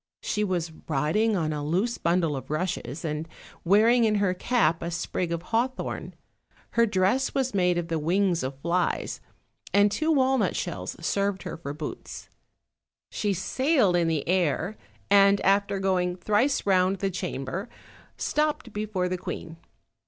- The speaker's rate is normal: Yes, average, 155 wpm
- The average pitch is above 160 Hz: Yes, medium, 185 Hz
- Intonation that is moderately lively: Yes, average, 3.8 semitones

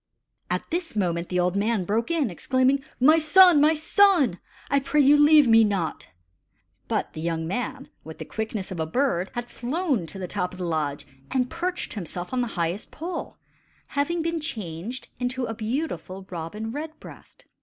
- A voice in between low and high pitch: No, high, 235 Hz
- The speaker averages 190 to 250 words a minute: No, average, 180 wpm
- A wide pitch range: Yes, wide, 8.5 semitones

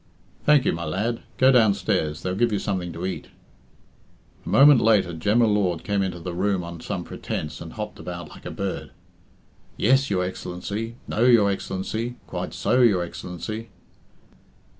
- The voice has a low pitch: Yes, low, 100 Hz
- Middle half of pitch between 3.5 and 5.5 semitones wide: Yes, average, 4.3 semitones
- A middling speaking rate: Yes, average, 165 wpm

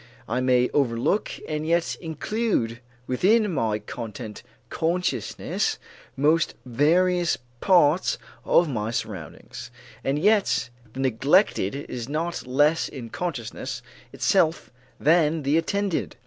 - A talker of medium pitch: Yes, medium, 150 Hz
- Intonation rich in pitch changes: Yes, wide, 5.8 semitones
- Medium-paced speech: No, slow, 110 wpm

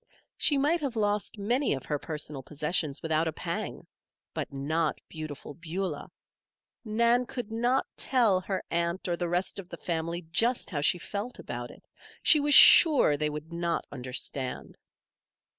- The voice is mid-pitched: Yes, medium, 175 Hz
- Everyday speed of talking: Yes, average, 160 wpm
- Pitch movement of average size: No, wide, 6.9 semitones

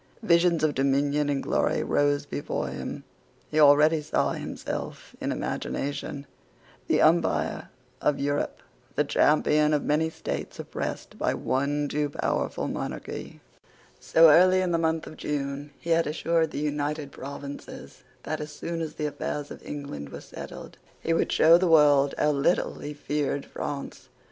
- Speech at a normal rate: Yes, average, 155 wpm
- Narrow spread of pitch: Yes, narrow, 2.0 semitones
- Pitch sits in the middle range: Yes, medium, 150 Hz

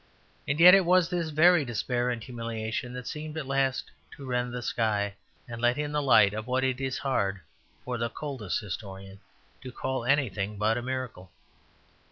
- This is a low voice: Yes, low, 125 Hz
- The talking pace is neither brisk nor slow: Yes, average, 185 wpm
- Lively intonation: No, average, 3.9 semitones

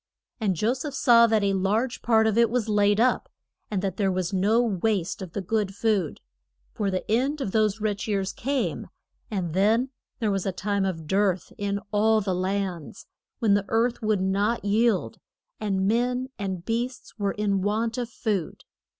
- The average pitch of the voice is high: Yes, high, 210 Hz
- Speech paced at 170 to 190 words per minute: Yes, average, 185 wpm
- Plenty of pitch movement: No, average, 2.9 semitones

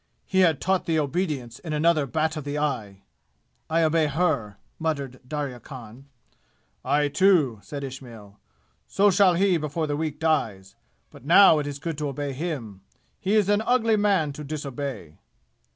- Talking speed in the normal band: Yes, average, 165 wpm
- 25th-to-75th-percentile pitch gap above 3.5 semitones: Yes, average, 3.9 semitones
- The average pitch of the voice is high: No, medium, 150 Hz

